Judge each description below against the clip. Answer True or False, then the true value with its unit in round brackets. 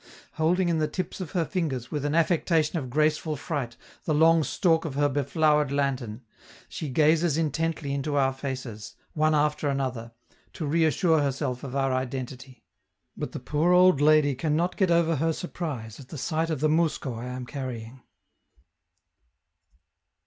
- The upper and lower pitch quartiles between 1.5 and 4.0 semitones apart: True (3.4 semitones)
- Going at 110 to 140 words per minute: False (165 wpm)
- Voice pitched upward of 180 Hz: False (150 Hz)